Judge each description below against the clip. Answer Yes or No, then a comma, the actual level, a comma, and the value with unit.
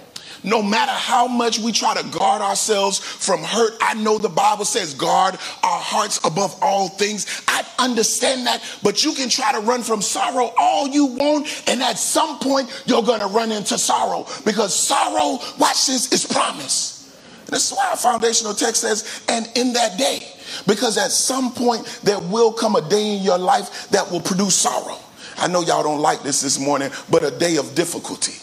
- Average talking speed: Yes, average, 190 wpm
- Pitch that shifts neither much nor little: Yes, average, 3.6 semitones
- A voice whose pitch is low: No, high, 230 Hz